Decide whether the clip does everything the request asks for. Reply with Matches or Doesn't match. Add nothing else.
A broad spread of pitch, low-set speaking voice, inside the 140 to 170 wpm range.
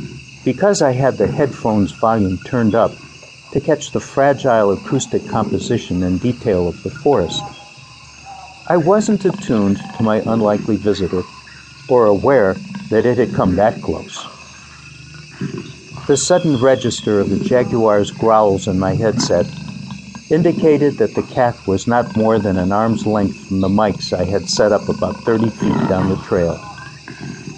Matches